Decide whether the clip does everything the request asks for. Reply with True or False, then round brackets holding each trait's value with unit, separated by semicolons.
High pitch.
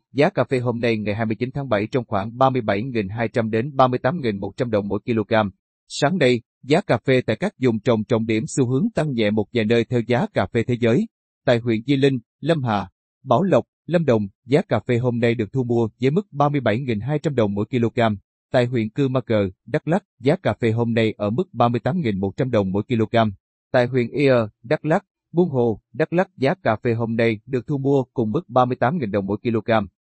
False (120 Hz)